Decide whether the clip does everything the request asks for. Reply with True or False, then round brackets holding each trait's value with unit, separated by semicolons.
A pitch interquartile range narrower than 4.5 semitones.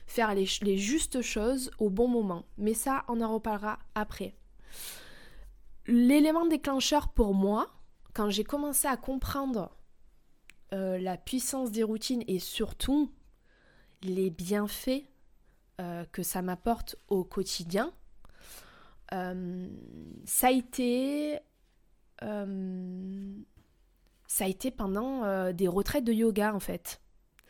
False (5.1 semitones)